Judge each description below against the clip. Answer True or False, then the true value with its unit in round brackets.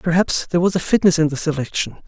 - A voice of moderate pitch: True (165 Hz)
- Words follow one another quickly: True (230 wpm)